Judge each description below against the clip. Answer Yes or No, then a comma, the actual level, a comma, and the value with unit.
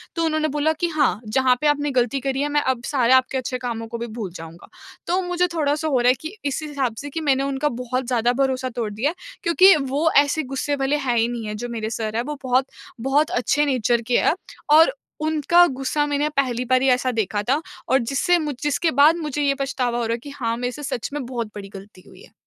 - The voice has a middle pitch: No, very high, 265 Hz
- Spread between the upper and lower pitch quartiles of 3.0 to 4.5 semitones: Yes, average, 3.6 semitones